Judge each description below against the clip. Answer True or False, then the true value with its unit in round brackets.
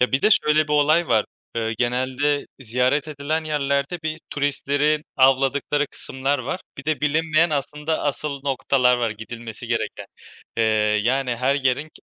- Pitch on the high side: False (140 Hz)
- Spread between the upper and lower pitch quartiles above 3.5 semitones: False (2.8 semitones)